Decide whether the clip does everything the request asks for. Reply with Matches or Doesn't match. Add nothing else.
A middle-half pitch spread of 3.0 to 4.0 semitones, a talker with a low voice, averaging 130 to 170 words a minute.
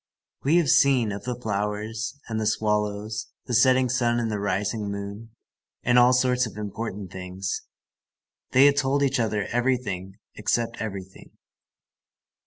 Matches